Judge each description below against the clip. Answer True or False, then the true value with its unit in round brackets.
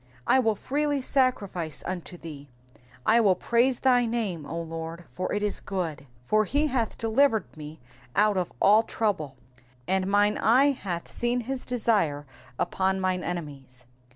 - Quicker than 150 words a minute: True (160 wpm)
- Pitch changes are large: True (6.0 semitones)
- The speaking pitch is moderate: False (200 Hz)